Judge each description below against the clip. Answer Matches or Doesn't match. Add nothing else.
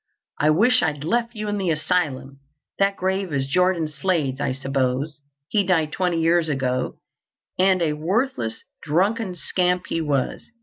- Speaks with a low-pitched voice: Doesn't match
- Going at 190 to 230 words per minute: Doesn't match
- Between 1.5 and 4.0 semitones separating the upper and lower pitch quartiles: Doesn't match